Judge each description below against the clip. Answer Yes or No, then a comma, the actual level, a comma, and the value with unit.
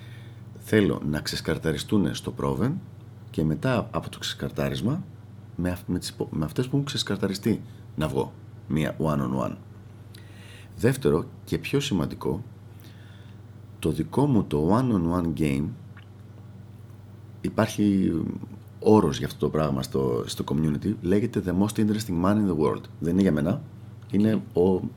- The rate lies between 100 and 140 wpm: Yes, average, 125 wpm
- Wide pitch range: No, average, 4.9 semitones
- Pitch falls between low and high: No, low, 105 Hz